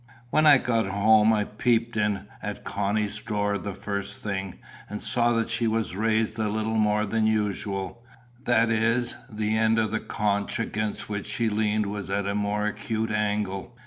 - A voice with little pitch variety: Yes, narrow, 1.6 semitones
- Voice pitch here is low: Yes, low, 105 Hz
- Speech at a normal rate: Yes, average, 175 wpm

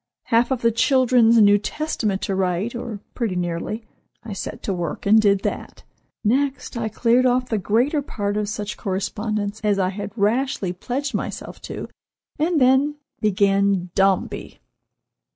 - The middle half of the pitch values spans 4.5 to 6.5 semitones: No, average, 3.8 semitones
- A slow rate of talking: No, average, 150 wpm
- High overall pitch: Yes, high, 215 Hz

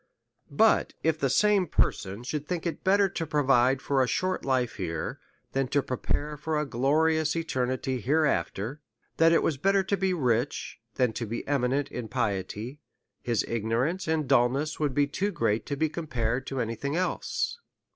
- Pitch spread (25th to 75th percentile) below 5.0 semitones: Yes, average, 4.6 semitones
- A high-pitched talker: No, medium, 140 Hz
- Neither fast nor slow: Yes, average, 175 wpm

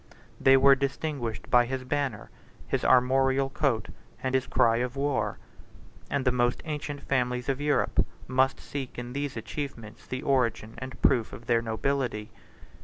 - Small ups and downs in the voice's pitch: Yes, narrow, 2.2 semitones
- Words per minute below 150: No, average, 155 wpm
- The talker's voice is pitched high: No, low, 130 Hz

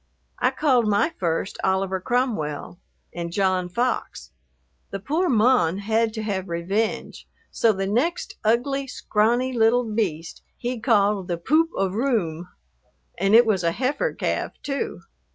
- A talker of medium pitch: No, high, 215 Hz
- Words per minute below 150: Yes, average, 140 wpm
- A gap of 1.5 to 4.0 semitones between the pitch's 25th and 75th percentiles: No, average, 4.7 semitones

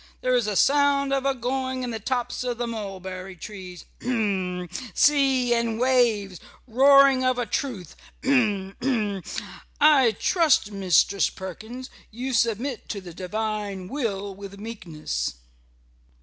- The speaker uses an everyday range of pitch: Yes, average, 4.7 semitones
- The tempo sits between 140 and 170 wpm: Yes, average, 145 wpm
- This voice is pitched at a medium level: No, high, 225 Hz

